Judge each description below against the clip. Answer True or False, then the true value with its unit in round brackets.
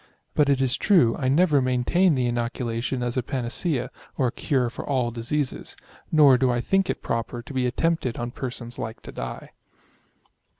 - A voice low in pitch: True (125 Hz)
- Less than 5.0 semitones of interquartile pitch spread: True (2.9 semitones)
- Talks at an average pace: True (180 wpm)